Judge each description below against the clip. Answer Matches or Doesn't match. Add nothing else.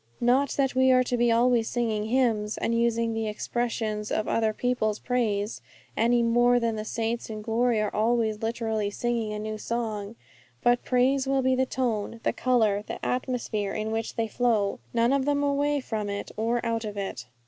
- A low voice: Doesn't match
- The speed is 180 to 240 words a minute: Matches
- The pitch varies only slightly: Matches